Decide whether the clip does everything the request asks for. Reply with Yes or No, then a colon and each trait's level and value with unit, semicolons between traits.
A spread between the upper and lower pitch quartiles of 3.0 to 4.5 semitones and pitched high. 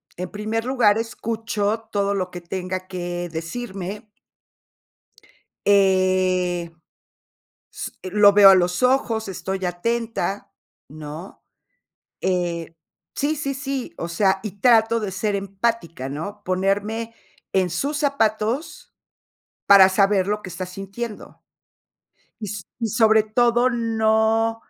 Yes: average, 3.4 semitones; high, 205 Hz